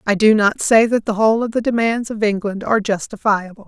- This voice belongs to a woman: Yes, female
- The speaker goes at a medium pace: No, fast, 230 wpm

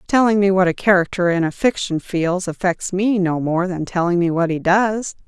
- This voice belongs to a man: No, female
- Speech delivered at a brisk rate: Yes, fast, 215 wpm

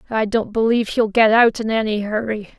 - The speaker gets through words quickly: Yes, fast, 210 wpm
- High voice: Yes, high, 220 Hz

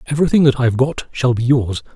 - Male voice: Yes, male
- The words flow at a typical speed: No, fast, 215 wpm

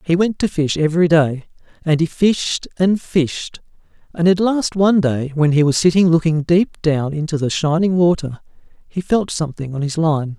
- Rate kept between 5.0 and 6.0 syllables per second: No, 4.8 syllables/s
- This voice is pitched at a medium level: Yes, medium, 165 Hz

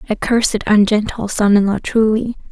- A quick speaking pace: No, average, 165 wpm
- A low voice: No, high, 215 Hz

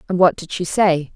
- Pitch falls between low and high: Yes, medium, 175 Hz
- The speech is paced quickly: Yes, fast, 260 wpm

